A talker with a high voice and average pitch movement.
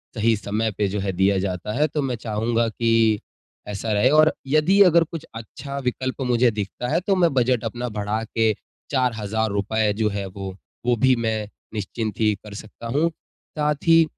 No: low, 115 Hz; average, 3.8 semitones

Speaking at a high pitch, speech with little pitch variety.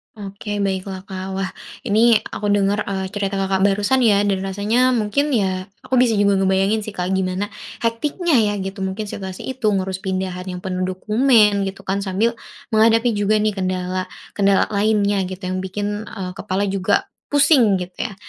Yes: high, 200 Hz; narrow, 2.2 semitones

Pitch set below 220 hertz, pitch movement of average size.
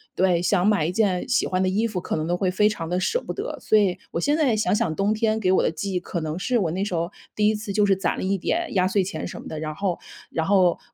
Yes: high, 190 Hz; average, 3.1 semitones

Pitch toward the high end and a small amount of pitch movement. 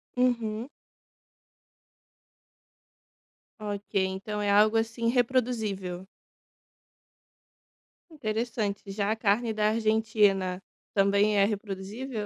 Yes: high, 215 Hz; narrow, 2.2 semitones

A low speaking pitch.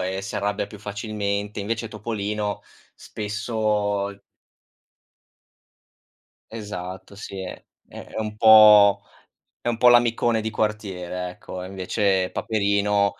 Yes: low, 105 Hz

